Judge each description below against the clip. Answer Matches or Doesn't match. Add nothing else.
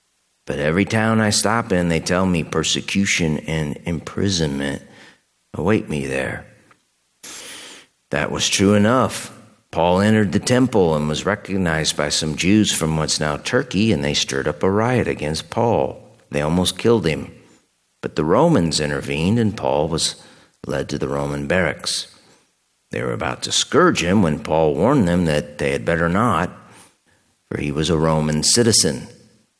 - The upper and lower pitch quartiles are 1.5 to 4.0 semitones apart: Doesn't match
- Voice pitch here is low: Matches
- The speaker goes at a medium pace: Matches